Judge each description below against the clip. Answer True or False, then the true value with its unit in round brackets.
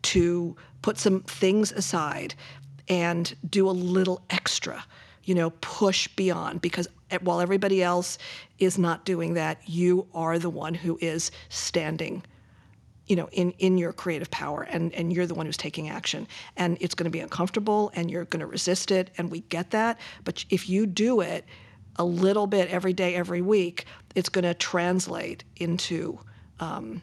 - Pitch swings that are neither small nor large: False (1.9 semitones)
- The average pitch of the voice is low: False (175 Hz)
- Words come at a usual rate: True (175 wpm)